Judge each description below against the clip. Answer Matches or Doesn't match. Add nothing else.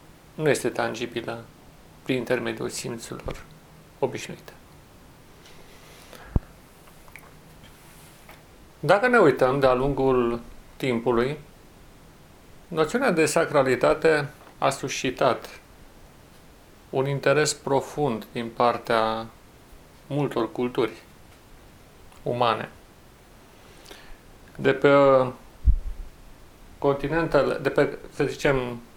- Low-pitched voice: Matches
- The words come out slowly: Matches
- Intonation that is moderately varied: Matches